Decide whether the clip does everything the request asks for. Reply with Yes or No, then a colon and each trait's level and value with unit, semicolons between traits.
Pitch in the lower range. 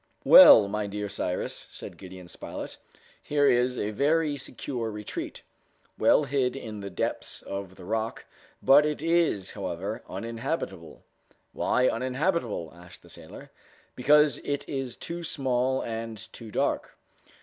Yes: low, 120 Hz